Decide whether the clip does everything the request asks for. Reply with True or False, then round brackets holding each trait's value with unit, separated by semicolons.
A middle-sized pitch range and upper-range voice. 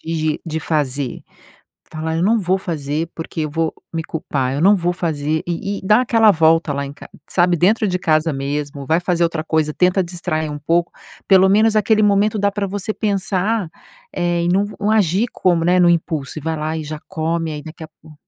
False (3.6 semitones; 170 Hz)